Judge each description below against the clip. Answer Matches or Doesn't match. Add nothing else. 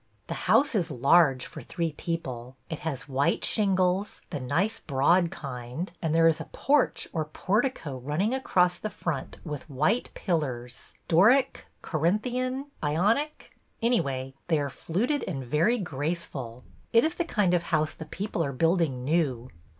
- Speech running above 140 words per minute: Matches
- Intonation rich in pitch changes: Matches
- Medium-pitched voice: Matches